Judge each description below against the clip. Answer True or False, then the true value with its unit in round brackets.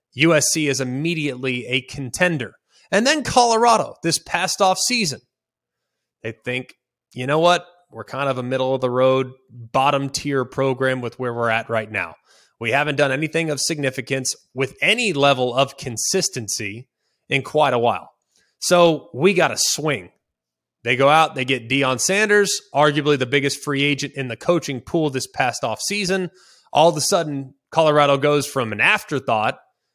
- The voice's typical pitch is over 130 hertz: True (140 Hz)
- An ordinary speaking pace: True (165 wpm)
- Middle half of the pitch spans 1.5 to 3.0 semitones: False (4.3 semitones)